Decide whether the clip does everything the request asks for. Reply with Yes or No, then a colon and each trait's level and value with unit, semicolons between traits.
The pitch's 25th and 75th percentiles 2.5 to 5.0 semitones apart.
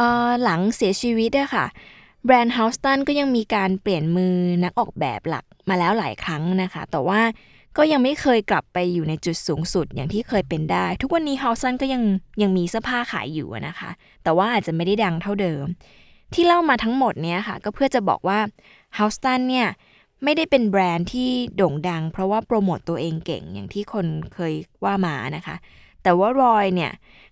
No: wide, 5.6 semitones